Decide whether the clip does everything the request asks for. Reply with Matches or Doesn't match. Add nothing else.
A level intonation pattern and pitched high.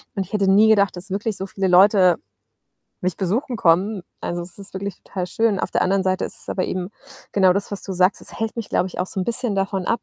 Matches